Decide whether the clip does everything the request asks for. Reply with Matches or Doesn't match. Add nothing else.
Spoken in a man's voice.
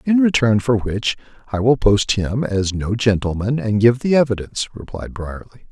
Matches